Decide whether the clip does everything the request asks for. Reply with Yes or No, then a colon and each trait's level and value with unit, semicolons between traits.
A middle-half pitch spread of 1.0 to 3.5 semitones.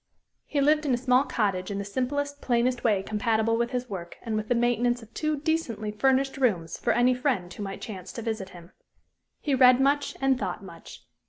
No: average, 4.2 semitones